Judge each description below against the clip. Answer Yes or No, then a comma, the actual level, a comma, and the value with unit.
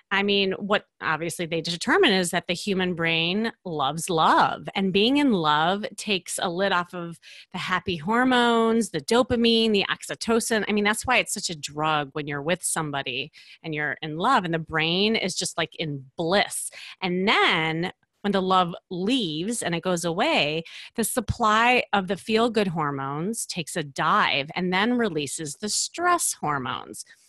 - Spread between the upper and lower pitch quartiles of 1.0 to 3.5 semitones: No, average, 4.8 semitones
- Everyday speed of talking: Yes, average, 175 wpm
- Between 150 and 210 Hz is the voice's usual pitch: Yes, medium, 185 Hz